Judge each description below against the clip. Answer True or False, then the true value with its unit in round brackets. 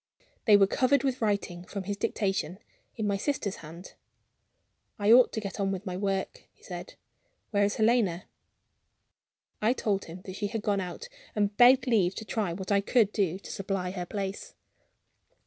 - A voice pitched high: True (200 Hz)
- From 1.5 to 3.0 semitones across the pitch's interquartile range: True (2.4 semitones)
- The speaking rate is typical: True (180 wpm)